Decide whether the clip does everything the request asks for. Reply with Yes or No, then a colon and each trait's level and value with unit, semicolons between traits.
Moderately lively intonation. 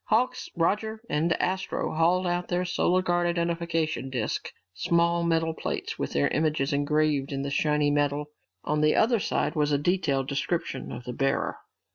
Yes: average, 3.4 semitones